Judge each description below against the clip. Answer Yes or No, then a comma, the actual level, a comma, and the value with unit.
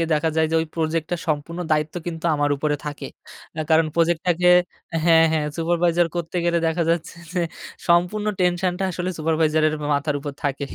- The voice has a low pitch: No, medium, 165 Hz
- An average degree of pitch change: No, narrow, 1.9 semitones